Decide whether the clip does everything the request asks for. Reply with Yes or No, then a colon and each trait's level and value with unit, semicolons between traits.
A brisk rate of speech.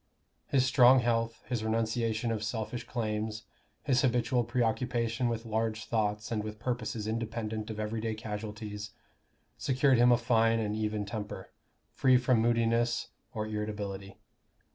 No: slow, 135 wpm